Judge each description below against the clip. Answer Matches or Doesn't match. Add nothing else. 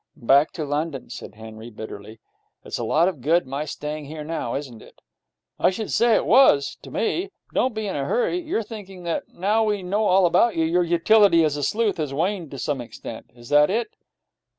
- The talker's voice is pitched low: Doesn't match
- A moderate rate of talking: Doesn't match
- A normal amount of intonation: Doesn't match